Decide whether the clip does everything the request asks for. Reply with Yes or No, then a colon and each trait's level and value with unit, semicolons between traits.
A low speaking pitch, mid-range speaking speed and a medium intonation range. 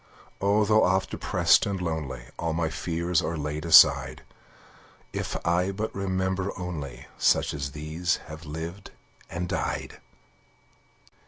No: very low, 85 Hz; slow, 130 wpm; average, 3.2 semitones